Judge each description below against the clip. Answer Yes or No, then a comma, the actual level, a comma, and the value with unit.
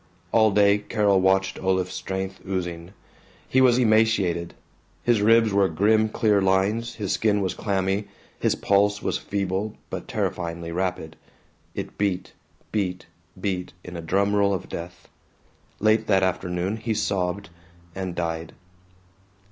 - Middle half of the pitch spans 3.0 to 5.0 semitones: No, narrow, 2.6 semitones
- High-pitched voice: No, very low, 95 Hz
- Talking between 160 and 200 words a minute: No, slow, 135 wpm